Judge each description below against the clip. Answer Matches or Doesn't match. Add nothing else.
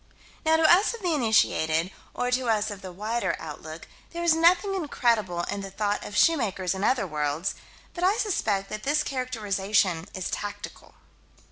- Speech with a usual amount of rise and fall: Doesn't match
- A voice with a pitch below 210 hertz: Doesn't match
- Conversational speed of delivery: Matches